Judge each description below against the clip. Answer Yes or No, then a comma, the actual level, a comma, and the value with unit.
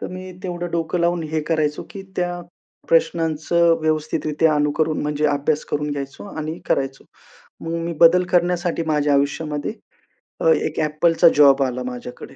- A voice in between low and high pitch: Yes, medium, 155 Hz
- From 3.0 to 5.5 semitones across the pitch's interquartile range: No, narrow, 2.5 semitones